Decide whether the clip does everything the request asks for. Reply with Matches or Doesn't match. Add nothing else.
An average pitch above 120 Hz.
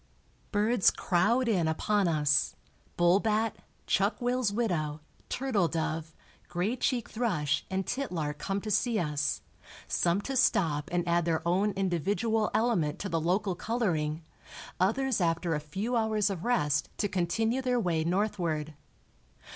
Matches